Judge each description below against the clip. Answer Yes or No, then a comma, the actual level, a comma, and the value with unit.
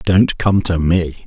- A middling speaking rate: Yes, average, 190 wpm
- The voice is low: Yes, very low, 90 Hz